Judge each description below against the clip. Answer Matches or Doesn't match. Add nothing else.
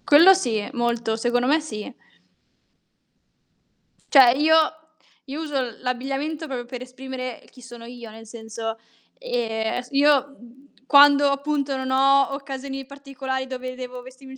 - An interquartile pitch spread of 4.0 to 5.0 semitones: Doesn't match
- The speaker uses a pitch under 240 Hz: Doesn't match